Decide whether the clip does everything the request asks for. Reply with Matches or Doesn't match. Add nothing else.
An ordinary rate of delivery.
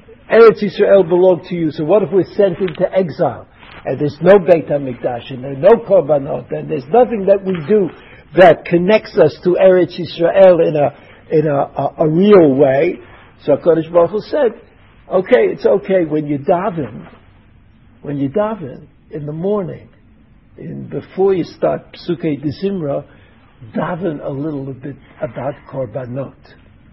Matches